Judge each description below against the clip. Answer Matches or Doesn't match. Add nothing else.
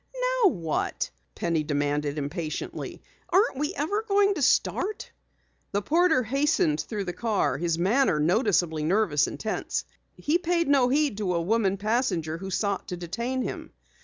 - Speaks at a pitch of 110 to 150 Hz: Doesn't match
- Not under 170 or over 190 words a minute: Doesn't match